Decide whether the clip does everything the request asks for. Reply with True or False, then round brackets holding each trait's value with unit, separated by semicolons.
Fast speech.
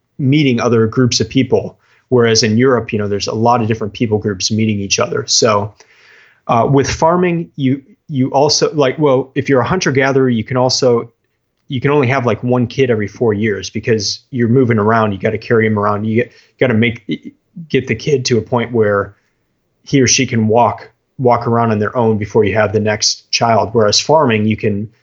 True (215 wpm)